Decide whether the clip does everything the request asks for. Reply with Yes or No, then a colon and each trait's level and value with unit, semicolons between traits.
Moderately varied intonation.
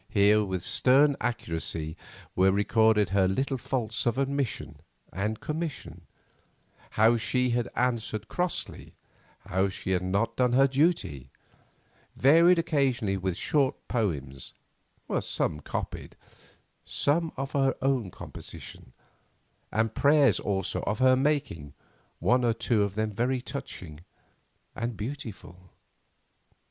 No: wide, 5.7 semitones